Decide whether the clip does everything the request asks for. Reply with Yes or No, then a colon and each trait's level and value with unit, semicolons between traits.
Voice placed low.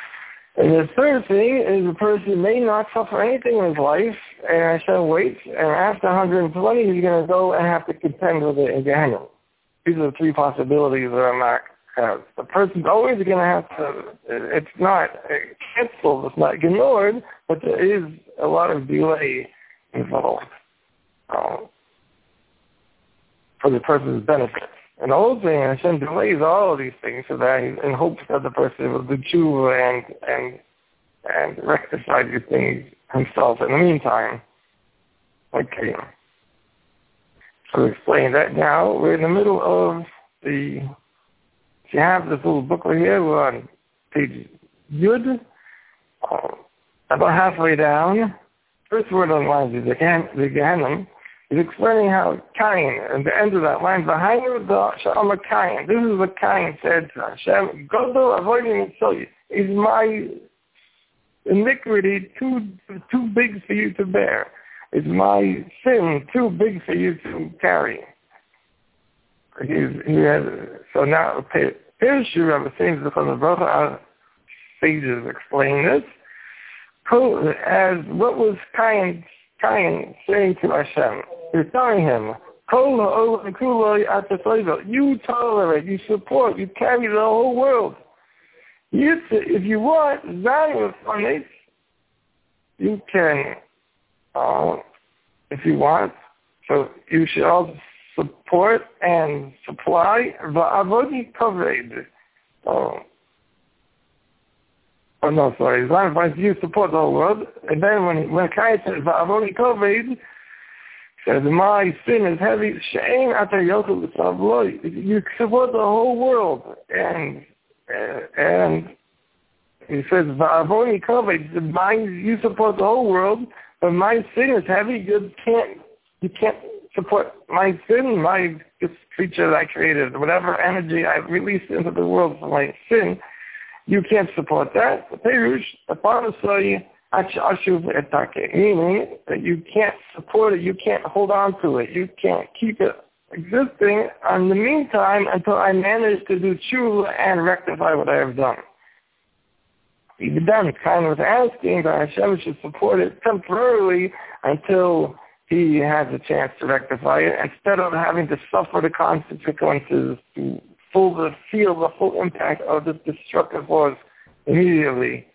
No: high, 195 Hz